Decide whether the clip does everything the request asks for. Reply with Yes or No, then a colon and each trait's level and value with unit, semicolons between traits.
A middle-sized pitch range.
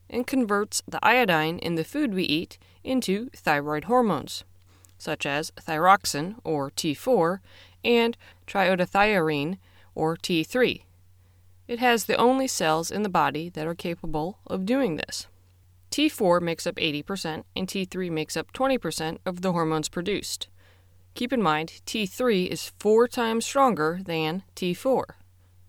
No: wide, 6.1 semitones